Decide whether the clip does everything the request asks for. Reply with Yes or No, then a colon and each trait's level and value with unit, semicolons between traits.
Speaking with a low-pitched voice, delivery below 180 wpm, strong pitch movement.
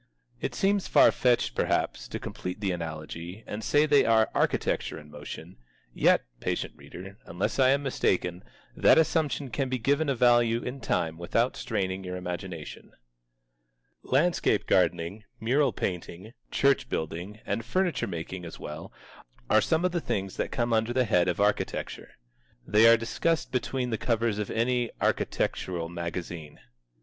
Yes: low, 110 Hz; average, 155 wpm; wide, 6.3 semitones